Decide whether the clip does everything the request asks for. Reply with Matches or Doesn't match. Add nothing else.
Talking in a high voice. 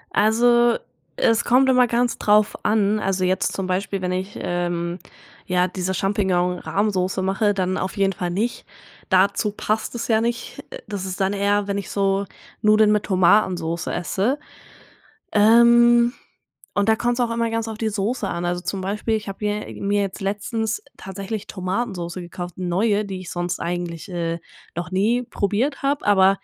Matches